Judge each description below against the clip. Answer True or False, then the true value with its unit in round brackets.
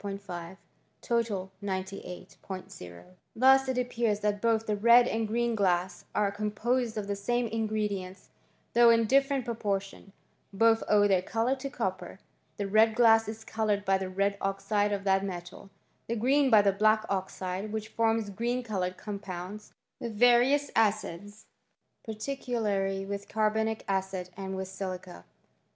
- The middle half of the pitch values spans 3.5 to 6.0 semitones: False (2.8 semitones)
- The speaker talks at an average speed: True (145 wpm)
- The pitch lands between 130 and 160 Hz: False (210 Hz)